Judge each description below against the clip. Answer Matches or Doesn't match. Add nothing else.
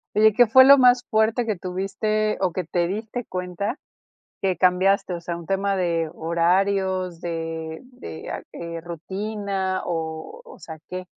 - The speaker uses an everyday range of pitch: Matches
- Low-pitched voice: Doesn't match